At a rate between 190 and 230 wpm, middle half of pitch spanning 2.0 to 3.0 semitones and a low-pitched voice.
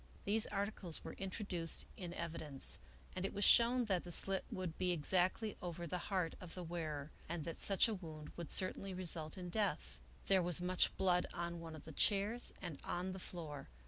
No: average, 195 wpm; average, 2.7 semitones; medium, 180 Hz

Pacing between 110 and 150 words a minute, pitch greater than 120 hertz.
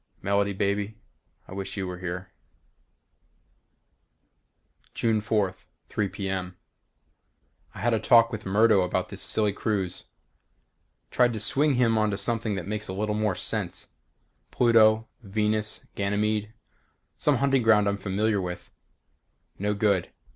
No: slow, 135 wpm; low, 105 Hz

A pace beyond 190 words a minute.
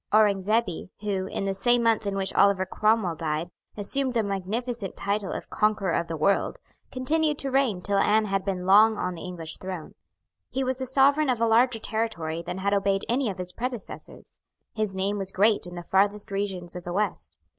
Yes: average, 200 wpm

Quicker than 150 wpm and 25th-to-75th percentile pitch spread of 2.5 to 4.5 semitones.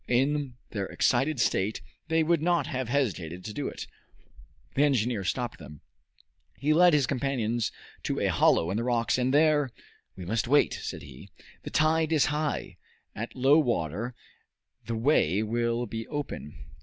No: average, 160 wpm; average, 4.9 semitones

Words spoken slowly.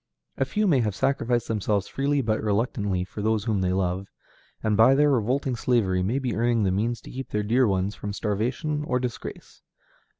No: average, 195 wpm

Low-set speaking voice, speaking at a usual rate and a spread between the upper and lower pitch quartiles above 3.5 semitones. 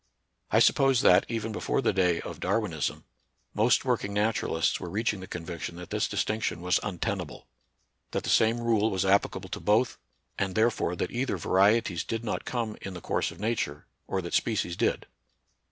Yes: low, 105 Hz; average, 180 wpm; average, 4.1 semitones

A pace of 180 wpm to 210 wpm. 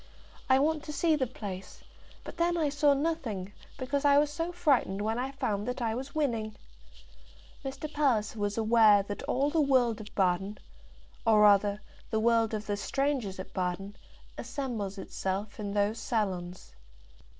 No: average, 160 wpm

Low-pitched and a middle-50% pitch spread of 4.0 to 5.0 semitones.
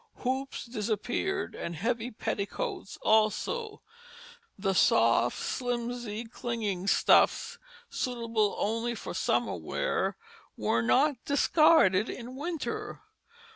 No: high, 235 Hz; average, 4.5 semitones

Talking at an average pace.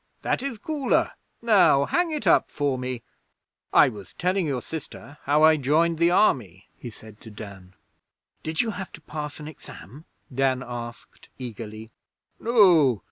Yes: average, 155 wpm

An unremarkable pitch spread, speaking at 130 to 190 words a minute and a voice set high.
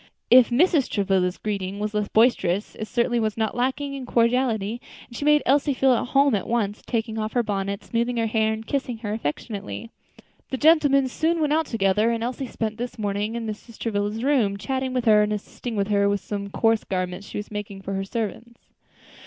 No: average, 3.4 semitones; average, 200 wpm; high, 225 Hz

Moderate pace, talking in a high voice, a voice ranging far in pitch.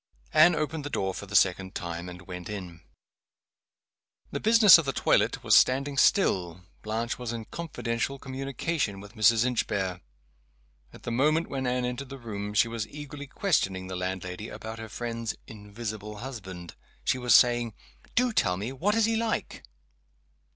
No: average, 165 wpm; low, 115 Hz; wide, 5.8 semitones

